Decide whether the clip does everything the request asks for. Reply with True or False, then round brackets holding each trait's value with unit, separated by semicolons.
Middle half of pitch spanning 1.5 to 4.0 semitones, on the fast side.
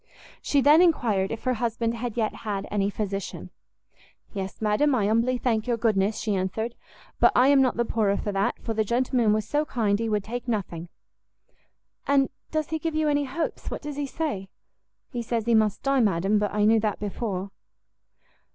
False (3.7 semitones; 195 wpm)